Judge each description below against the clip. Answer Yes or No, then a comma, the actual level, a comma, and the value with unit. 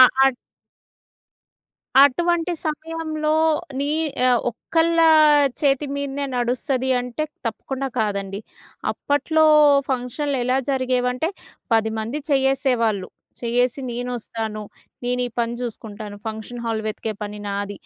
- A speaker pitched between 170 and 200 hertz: No, very high, 250 Hz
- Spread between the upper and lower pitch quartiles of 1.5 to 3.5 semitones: No, average, 4.0 semitones